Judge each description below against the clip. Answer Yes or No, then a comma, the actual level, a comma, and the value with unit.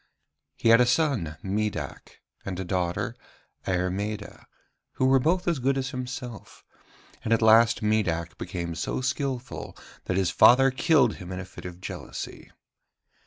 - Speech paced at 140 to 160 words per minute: Yes, average, 150 wpm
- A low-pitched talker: Yes, low, 110 Hz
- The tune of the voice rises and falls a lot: Yes, wide, 6.0 semitones